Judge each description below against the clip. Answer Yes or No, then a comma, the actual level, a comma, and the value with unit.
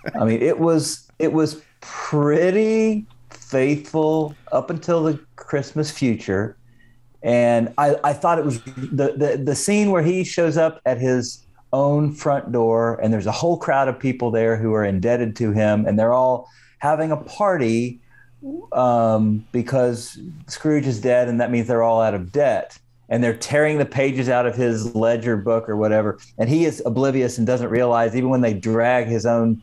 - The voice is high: No, low, 125 Hz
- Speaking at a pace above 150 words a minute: Yes, average, 180 wpm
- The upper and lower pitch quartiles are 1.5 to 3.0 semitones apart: No, average, 4.4 semitones